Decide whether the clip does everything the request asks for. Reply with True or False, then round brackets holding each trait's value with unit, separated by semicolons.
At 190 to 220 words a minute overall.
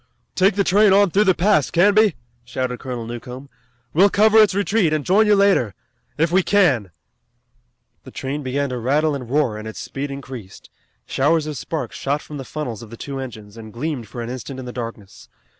True (200 wpm)